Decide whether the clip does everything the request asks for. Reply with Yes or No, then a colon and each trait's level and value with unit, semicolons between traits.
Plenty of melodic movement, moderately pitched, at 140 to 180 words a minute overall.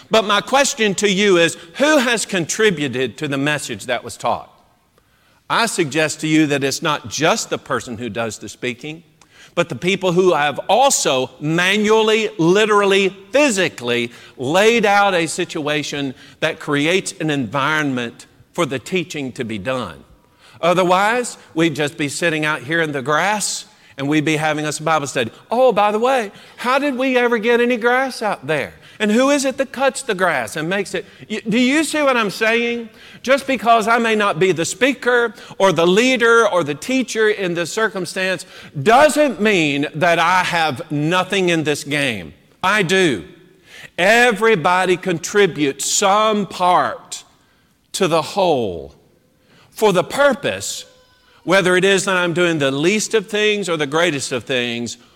Yes: wide, 6.3 semitones; medium, 180 Hz; average, 165 wpm